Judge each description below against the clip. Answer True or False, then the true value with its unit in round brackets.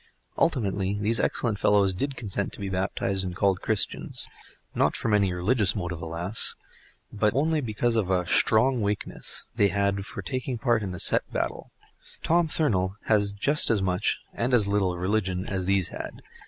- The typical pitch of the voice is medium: False (100 Hz)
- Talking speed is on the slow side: False (165 wpm)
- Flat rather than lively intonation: False (3.3 semitones)